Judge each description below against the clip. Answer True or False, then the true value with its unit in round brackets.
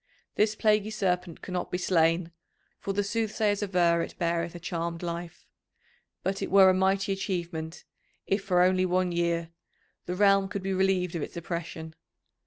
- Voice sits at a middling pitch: True (180 Hz)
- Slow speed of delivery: False (165 wpm)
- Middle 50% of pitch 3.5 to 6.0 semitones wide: False (2.4 semitones)